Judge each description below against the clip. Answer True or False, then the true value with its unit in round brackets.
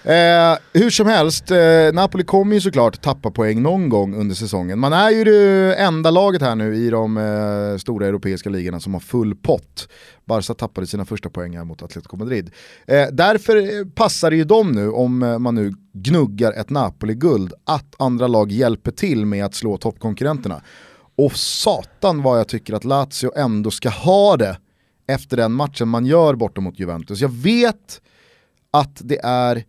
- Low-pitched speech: True (120 Hz)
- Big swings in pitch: True (7.4 semitones)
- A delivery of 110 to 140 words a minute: False (175 wpm)